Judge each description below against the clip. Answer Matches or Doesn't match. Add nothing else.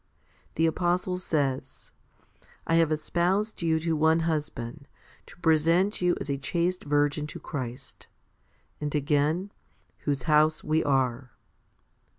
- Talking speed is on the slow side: Matches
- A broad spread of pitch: Doesn't match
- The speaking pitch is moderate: Matches